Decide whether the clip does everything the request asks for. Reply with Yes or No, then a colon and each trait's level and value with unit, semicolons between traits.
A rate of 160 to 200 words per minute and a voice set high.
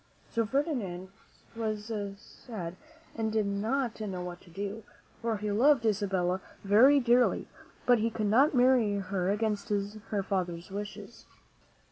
No: slow, 135 wpm; high, 210 Hz